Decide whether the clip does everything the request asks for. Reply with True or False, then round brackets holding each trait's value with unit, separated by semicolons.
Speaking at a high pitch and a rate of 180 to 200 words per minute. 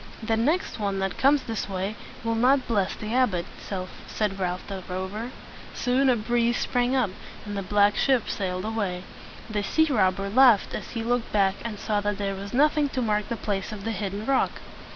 True (215 Hz; 195 wpm)